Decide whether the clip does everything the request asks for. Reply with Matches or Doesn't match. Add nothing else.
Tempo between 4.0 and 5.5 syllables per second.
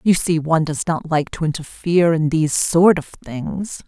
Matches